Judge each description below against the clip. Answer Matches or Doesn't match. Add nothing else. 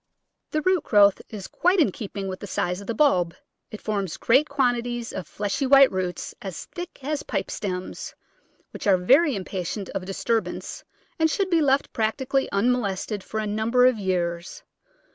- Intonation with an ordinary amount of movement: Doesn't match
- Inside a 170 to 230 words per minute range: Matches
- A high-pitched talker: Matches